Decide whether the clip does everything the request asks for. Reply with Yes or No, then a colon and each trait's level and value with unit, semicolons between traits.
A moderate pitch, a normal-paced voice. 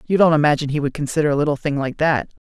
No: medium, 150 Hz; fast, 270 wpm